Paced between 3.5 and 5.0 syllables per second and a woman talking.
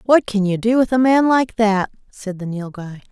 Yes: 4.7 syllables/s; female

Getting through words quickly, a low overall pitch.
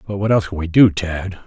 Yes: fast, 285 wpm; very low, 95 Hz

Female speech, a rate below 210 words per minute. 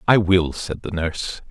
No: male; average, 200 wpm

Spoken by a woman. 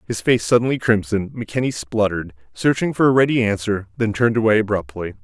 No: male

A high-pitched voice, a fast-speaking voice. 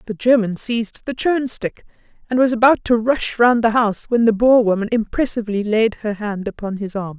Yes: high, 225 Hz; fast, 210 wpm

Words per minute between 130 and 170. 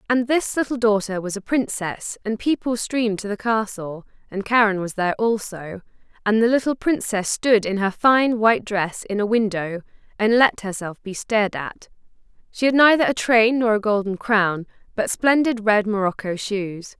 No: average, 180 wpm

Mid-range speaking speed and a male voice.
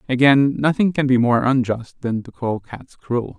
Yes: average, 195 wpm; male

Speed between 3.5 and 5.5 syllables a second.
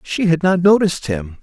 Yes: 5.3 syllables/s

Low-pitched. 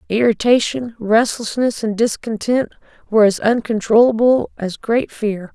No: high, 225 Hz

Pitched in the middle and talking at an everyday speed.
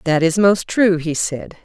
No: medium, 175 Hz; fast, 220 wpm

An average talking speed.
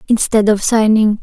Yes: average, 145 wpm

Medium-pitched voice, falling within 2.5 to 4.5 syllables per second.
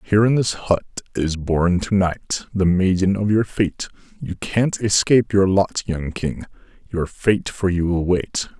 No: very low, 95 Hz; 4.2 syllables/s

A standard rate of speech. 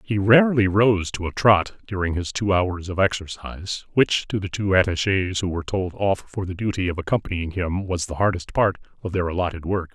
No: fast, 210 wpm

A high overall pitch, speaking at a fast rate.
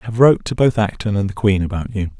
No: low, 105 Hz; fast, 300 wpm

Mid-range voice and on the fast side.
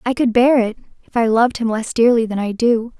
No: high, 230 Hz; fast, 260 wpm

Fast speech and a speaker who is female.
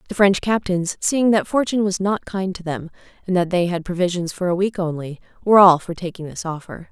Yes: fast, 225 wpm; female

